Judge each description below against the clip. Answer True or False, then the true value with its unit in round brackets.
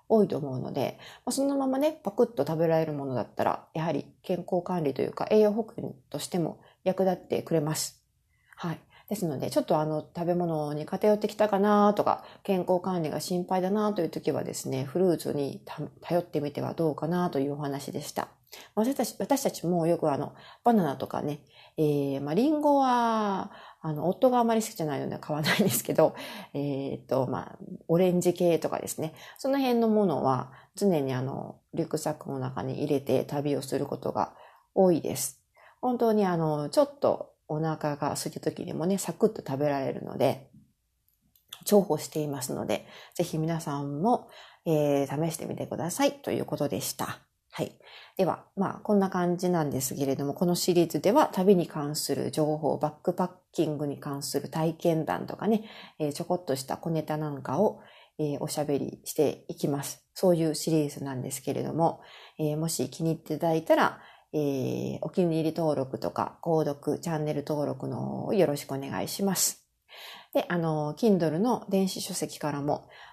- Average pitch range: True (4.7 semitones)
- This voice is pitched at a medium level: True (160 Hz)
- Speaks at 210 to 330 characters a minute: False (360 characters per minute)